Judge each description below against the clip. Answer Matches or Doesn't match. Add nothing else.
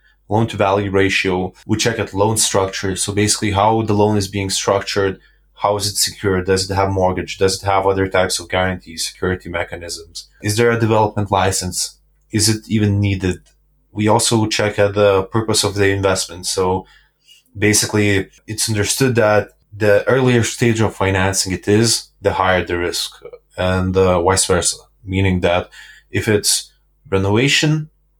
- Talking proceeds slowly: Doesn't match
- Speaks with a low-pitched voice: Matches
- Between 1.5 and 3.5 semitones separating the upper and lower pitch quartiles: Matches